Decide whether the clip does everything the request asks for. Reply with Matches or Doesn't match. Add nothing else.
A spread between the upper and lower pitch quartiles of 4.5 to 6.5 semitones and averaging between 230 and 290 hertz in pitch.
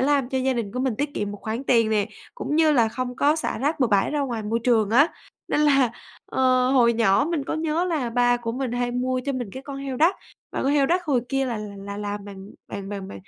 Doesn't match